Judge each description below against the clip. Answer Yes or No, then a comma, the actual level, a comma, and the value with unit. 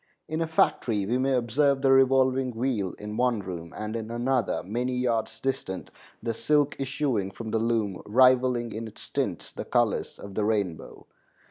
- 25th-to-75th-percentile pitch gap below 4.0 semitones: Yes, average, 3.6 semitones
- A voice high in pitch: No, low, 120 Hz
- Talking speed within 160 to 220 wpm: Yes, average, 170 wpm